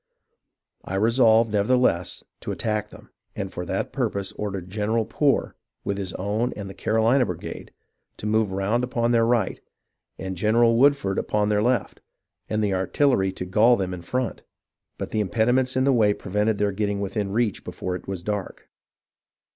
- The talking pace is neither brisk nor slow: Yes, average, 170 wpm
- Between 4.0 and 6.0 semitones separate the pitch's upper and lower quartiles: No, average, 3.2 semitones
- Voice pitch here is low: Yes, low, 105 Hz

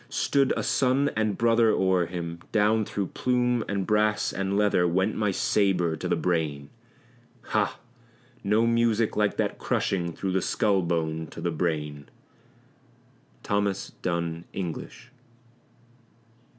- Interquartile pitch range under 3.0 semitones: No, average, 4.1 semitones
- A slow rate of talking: Yes, slow, 130 wpm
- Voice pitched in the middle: No, very low, 95 Hz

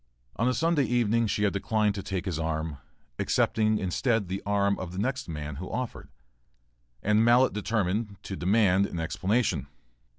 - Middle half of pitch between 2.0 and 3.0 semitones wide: No, average, 3.9 semitones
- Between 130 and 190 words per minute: Yes, average, 165 wpm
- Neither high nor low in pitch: No, low, 100 Hz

